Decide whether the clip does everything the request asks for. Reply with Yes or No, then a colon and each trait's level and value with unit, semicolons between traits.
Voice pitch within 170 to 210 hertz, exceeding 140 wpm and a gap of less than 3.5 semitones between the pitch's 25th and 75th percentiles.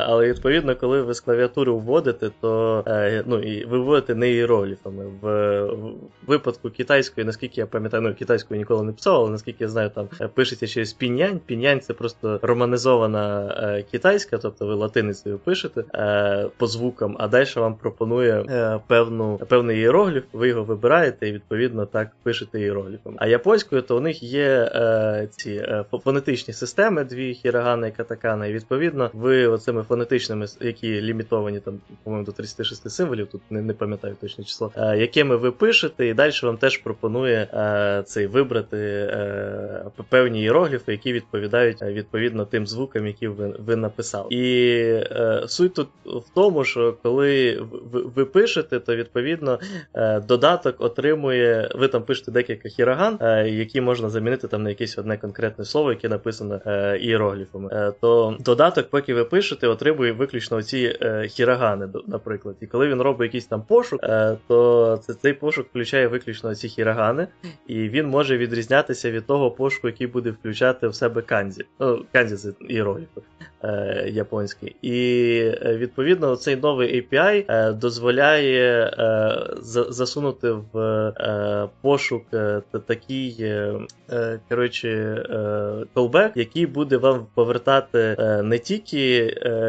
No: low, 115 Hz; average, 150 wpm; average, 2.9 semitones